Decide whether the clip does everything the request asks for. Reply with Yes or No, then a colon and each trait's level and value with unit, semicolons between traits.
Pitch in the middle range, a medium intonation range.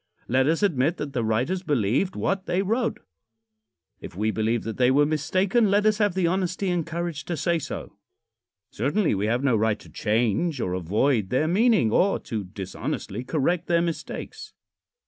No: medium, 150 Hz; wide, 8.2 semitones